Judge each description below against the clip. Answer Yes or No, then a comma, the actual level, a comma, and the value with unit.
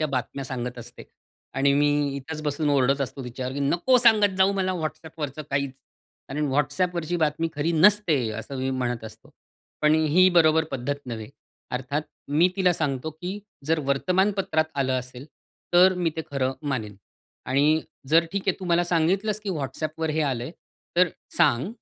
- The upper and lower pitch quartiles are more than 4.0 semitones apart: Yes, average, 4.6 semitones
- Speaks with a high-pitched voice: No, medium, 150 Hz